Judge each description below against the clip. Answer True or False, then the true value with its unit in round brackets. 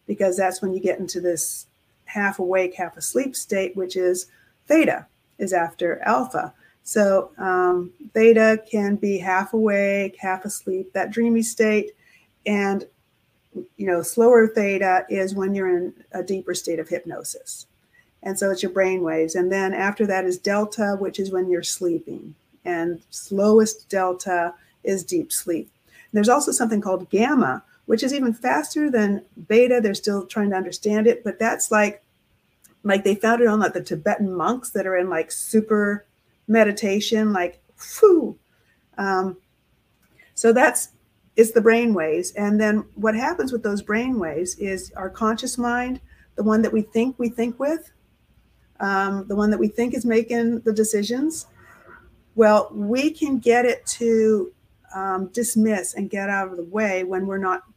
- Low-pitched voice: False (205 Hz)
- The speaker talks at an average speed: True (165 wpm)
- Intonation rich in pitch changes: False (3.4 semitones)